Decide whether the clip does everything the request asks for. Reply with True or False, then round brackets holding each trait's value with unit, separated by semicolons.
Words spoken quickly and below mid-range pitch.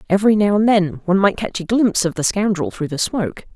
False (255 wpm; 190 Hz)